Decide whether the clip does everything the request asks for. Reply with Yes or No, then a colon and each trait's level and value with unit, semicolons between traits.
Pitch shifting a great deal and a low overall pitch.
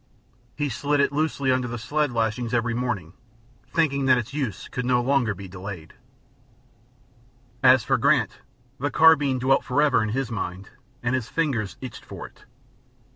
No: average, 3.7 semitones; low, 125 Hz